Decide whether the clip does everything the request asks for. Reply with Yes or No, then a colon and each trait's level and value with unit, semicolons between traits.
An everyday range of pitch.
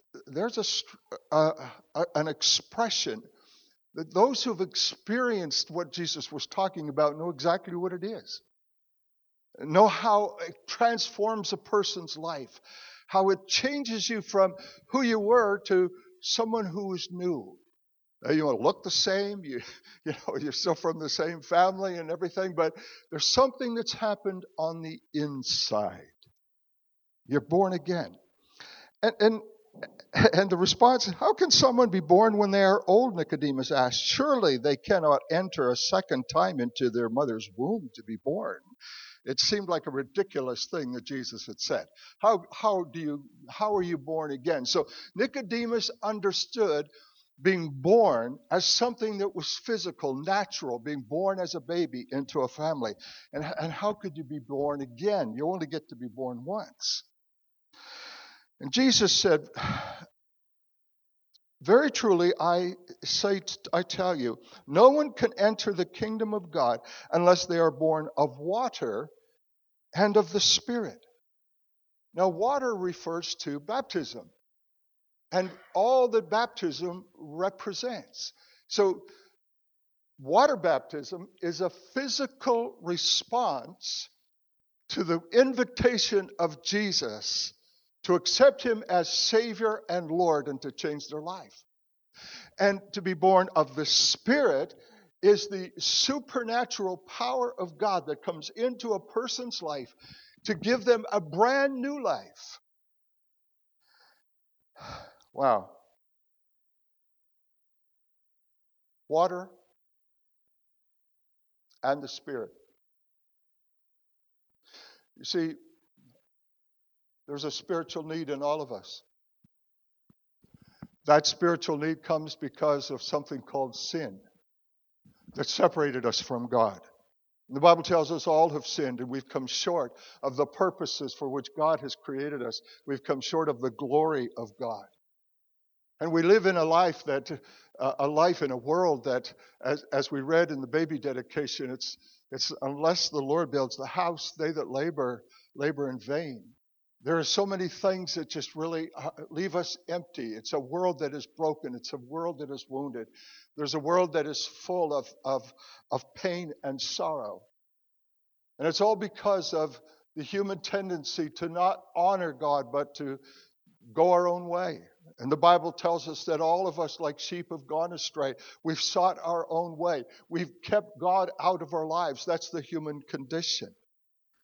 No: wide, 5.7 semitones